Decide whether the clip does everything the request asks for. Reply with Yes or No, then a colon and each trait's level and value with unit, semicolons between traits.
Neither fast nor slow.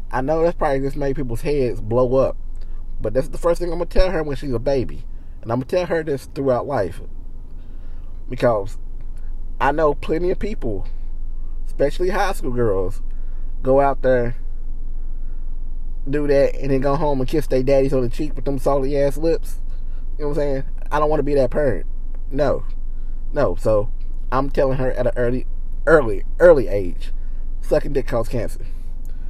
Yes: average, 180 wpm